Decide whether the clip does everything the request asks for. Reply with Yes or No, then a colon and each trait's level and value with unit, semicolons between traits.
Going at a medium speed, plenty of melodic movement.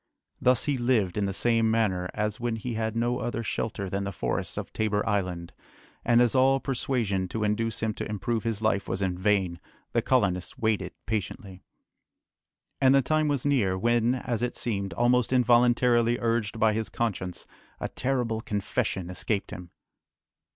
No: average, 170 wpm; average, 3.3 semitones